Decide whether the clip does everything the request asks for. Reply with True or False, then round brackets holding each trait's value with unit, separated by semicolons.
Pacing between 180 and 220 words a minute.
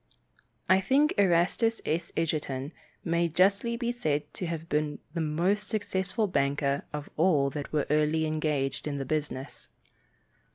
False (140 wpm)